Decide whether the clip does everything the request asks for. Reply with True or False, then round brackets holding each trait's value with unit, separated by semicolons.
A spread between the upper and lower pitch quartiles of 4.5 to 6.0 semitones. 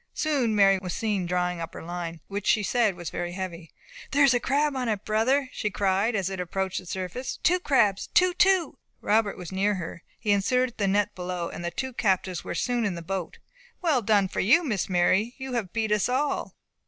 True (5.1 semitones)